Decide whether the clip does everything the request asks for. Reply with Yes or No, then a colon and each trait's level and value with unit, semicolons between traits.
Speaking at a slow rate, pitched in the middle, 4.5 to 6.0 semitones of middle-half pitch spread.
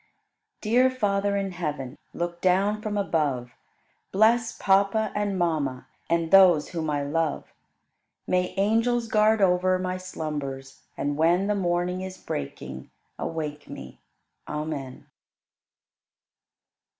Yes: slow, 115 wpm; medium, 180 Hz; average, 4.9 semitones